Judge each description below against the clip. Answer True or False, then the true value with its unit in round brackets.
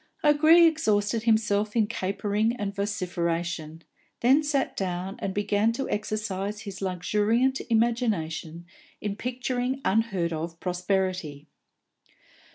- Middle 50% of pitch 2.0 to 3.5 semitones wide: False (4.2 semitones)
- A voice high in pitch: True (205 Hz)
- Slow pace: True (105 wpm)